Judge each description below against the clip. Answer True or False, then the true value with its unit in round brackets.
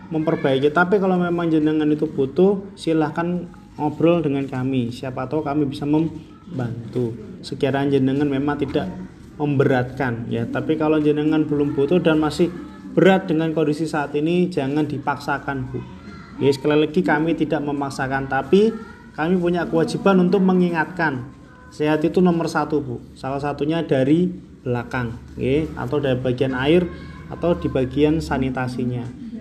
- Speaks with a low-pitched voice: False (150 Hz)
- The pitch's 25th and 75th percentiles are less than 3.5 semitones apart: True (3.0 semitones)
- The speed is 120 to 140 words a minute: True (135 wpm)